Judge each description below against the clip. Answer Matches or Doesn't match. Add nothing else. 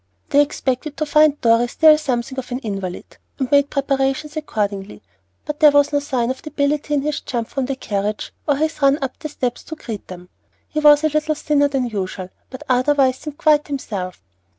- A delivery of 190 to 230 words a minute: Matches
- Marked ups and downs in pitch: Doesn't match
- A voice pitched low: Doesn't match